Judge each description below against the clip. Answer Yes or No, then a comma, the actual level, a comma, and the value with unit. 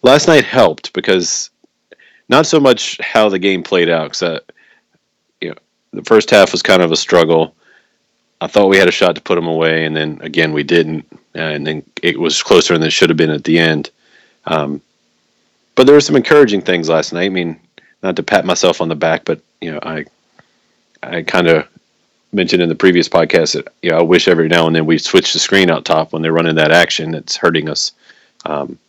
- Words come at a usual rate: No, fast, 220 wpm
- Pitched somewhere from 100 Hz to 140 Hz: No, very low, 80 Hz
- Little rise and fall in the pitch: Yes, narrow, 1.3 semitones